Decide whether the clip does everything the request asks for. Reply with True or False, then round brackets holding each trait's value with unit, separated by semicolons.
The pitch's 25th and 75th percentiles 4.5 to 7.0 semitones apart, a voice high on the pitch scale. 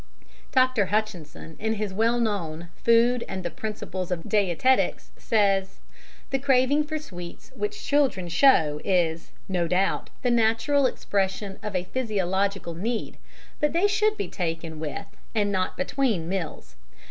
True (5.6 semitones; 205 Hz)